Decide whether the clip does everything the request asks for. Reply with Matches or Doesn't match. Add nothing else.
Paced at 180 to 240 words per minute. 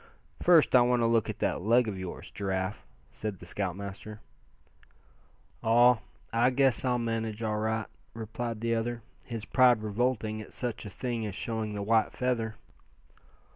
Doesn't match